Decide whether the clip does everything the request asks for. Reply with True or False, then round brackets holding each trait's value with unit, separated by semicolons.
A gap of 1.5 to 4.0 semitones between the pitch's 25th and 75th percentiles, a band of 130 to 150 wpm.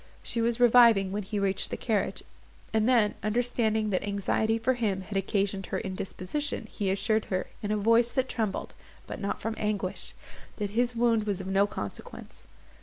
False (2.8 semitones; 180 wpm)